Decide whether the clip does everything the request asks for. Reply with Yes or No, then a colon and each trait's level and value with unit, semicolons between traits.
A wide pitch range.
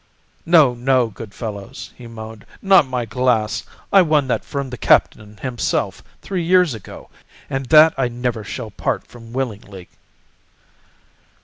No: average, 3.8 semitones